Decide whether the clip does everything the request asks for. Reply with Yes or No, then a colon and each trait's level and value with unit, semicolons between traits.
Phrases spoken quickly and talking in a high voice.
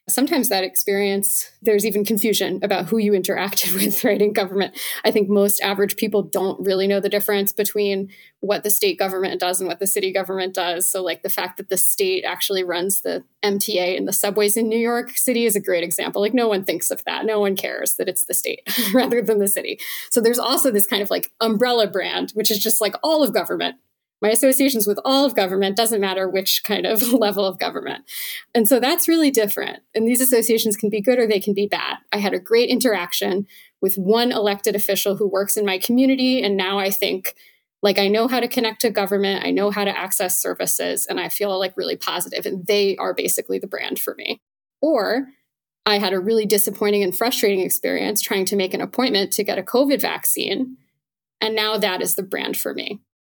Yes: fast, 220 wpm; high, 205 Hz